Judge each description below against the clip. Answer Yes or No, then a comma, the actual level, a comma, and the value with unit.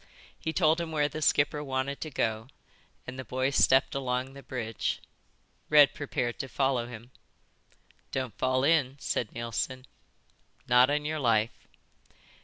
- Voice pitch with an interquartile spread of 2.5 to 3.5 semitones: Yes, average, 2.8 semitones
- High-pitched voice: No, low, 130 Hz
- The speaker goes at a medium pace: Yes, average, 145 wpm